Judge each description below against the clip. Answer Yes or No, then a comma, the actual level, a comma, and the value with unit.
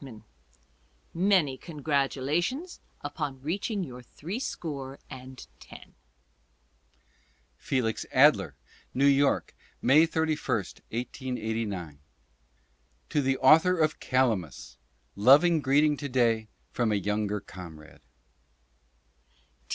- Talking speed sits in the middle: No, slow, 95 wpm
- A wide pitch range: Yes, wide, 5.7 semitones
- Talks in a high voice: No, low, 135 Hz